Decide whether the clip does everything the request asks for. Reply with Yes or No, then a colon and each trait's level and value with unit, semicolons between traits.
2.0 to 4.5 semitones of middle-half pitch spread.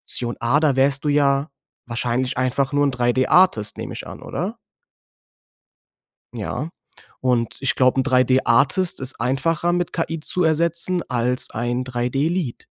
Yes: average, 3.8 semitones